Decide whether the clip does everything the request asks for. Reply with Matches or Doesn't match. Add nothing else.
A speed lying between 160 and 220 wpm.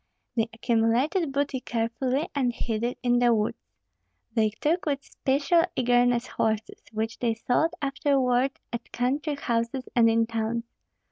Doesn't match